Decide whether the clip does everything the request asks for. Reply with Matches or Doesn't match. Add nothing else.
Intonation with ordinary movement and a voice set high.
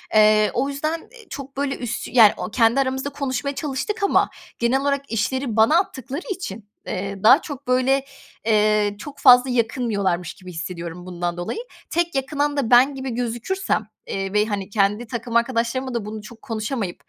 Matches